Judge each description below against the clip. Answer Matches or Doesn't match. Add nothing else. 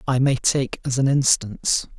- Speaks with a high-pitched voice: Doesn't match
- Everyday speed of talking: Matches